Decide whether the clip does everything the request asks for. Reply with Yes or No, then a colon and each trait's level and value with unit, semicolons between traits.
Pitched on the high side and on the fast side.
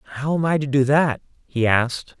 No: low, 135 Hz; fast, 220 wpm